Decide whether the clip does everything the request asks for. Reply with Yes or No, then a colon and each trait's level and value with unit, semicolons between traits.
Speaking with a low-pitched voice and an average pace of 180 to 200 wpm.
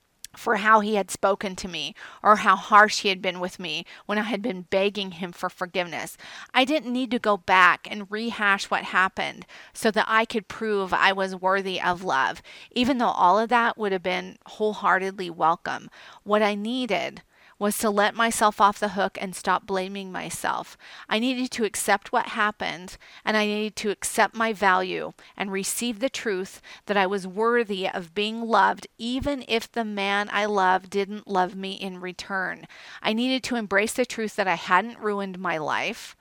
No: high, 205 Hz; average, 190 wpm